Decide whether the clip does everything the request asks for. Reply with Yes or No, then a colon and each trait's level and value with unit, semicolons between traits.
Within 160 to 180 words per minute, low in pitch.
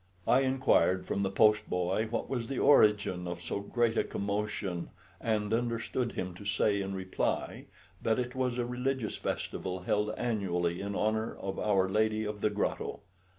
Yes: average, 170 wpm; low, 105 Hz